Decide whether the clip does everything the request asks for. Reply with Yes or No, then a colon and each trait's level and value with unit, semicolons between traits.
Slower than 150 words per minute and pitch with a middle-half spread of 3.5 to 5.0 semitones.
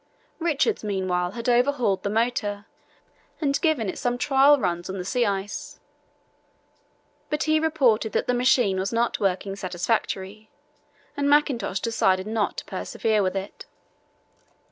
No: average, 140 wpm; wide, 5.4 semitones